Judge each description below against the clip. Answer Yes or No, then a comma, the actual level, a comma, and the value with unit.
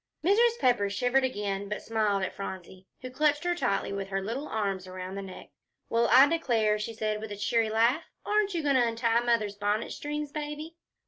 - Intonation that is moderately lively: No, wide, 5.9 semitones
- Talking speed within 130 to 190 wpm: No, average, 200 wpm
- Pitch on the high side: Yes, high, 230 Hz